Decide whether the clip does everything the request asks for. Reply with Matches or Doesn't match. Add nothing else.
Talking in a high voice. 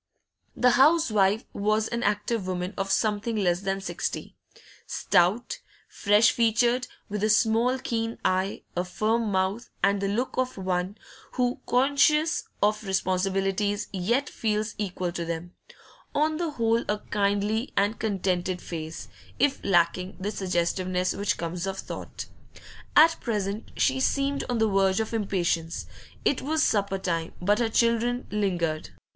Matches